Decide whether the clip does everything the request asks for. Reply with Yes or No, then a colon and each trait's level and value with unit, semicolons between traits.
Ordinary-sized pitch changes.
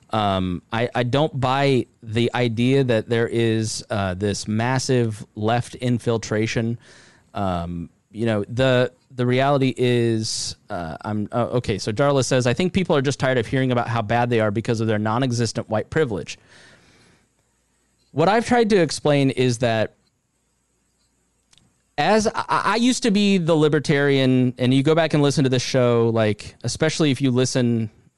Yes: average, 3.3 semitones